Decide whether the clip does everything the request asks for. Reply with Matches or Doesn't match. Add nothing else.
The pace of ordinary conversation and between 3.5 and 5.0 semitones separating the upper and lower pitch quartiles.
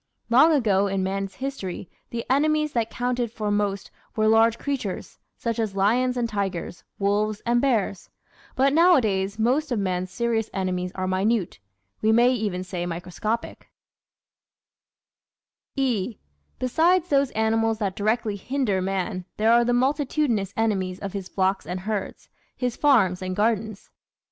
Matches